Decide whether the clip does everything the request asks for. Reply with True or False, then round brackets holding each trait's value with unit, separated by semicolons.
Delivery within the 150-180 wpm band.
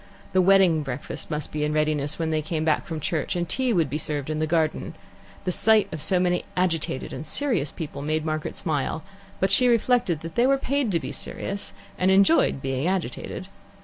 False (205 wpm)